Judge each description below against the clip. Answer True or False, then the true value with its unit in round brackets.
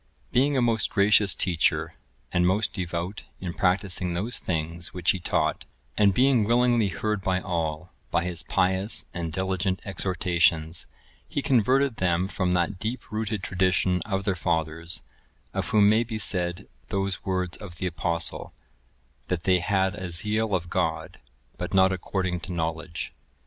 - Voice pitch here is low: True (95 Hz)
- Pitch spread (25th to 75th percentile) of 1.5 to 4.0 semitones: True (3.0 semitones)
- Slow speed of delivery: False (155 wpm)